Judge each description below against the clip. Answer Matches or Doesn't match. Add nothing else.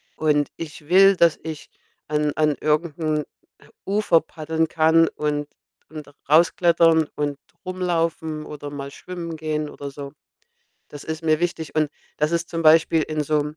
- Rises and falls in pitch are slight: Matches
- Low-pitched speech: Doesn't match